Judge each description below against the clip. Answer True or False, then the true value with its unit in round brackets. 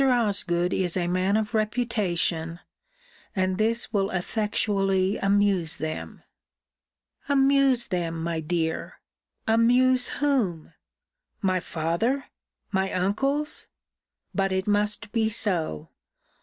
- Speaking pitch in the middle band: False (200 Hz)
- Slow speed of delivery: True (100 wpm)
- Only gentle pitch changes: False (4.5 semitones)